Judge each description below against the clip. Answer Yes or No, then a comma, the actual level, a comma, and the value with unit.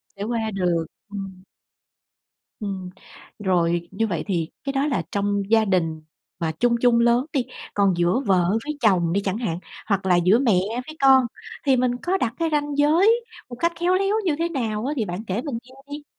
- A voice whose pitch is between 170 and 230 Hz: Yes, high, 220 Hz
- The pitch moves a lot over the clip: Yes, wide, 6.7 semitones